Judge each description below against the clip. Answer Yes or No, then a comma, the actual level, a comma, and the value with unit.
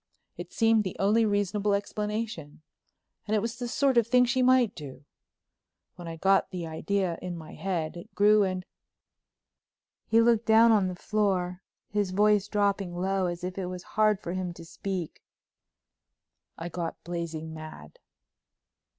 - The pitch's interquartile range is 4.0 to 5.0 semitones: No, average, 3.5 semitones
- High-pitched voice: Yes, high, 195 Hz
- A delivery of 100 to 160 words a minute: Yes, average, 155 wpm